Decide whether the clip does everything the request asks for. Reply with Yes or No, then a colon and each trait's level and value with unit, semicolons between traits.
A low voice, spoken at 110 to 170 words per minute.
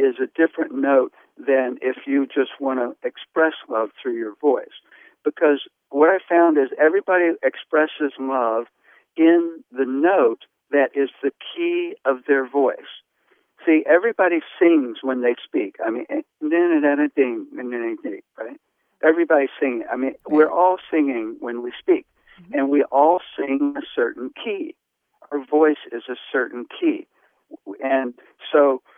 No: medium, 165 Hz; average, 140 wpm